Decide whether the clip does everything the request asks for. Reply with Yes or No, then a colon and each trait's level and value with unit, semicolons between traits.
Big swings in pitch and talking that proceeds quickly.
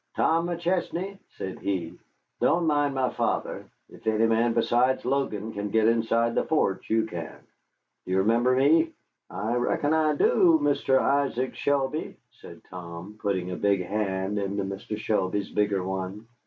No: wide, 6.0 semitones; average, 155 wpm